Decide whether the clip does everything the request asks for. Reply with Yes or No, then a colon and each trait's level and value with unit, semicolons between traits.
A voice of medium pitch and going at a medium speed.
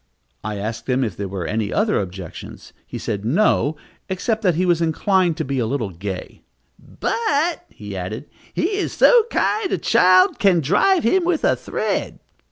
Yes: medium, 160 Hz; average, 175 wpm